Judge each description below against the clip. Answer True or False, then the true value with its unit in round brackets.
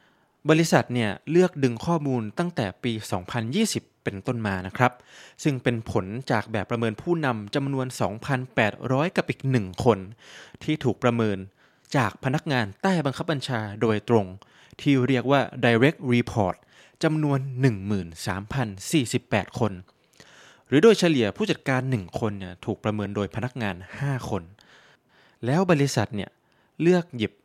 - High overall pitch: False (125 Hz)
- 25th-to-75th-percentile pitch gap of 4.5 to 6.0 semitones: True (4.9 semitones)